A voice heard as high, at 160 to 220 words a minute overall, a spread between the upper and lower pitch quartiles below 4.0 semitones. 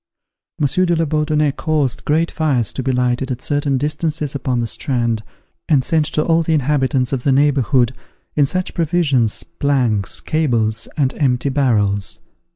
No: medium, 140 Hz; average, 165 wpm; average, 3.6 semitones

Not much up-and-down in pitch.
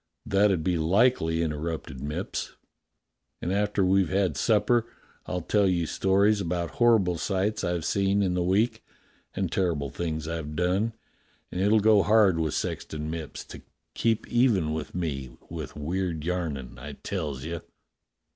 No: average, 4.1 semitones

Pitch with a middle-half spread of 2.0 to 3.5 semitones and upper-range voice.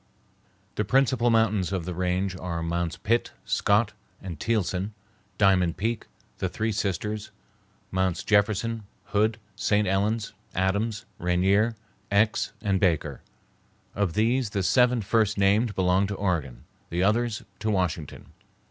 No: average, 3.1 semitones; low, 100 Hz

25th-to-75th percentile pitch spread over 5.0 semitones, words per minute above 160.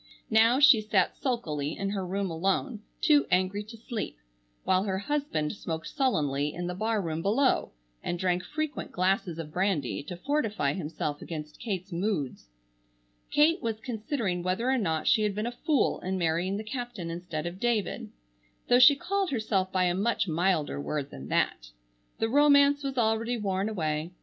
Yes: wide, 5.6 semitones; average, 170 wpm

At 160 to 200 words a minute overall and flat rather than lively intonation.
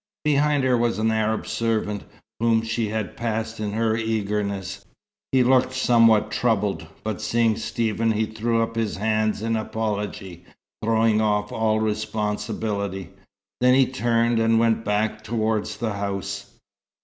No: average, 140 wpm; narrow, 1.5 semitones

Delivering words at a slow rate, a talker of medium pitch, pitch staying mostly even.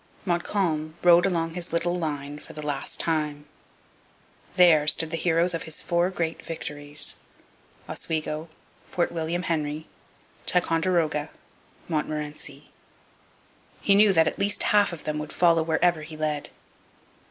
Yes: slow, 130 wpm; medium, 160 Hz; narrow, 2.3 semitones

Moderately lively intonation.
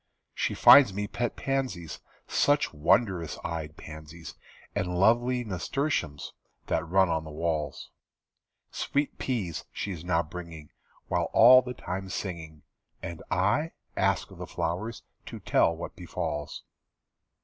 No: wide, 6.5 semitones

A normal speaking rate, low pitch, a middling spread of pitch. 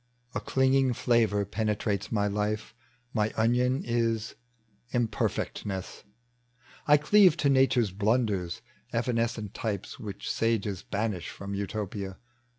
No: slow, 110 wpm; low, 110 Hz; average, 3.1 semitones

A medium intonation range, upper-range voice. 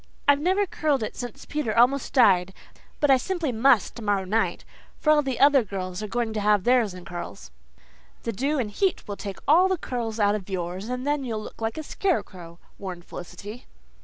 No: wide, 6.0 semitones; high, 225 Hz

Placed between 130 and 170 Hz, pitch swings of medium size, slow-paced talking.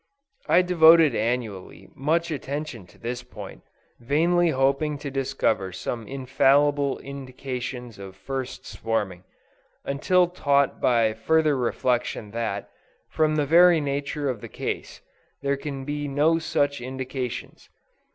Yes: low, 135 Hz; average, 3.6 semitones; slow, 120 wpm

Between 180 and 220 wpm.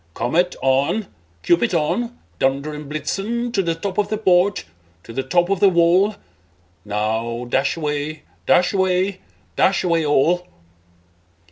No: average, 140 wpm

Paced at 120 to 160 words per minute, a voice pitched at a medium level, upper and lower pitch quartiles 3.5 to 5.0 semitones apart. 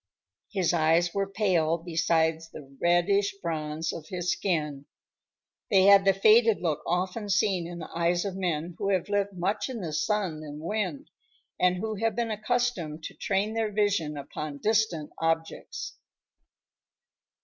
Yes: average, 150 wpm; medium, 180 Hz; average, 4.0 semitones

